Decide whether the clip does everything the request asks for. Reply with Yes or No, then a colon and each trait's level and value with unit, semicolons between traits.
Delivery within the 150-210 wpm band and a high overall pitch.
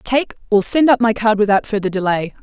No: fast, 225 wpm; high, 215 Hz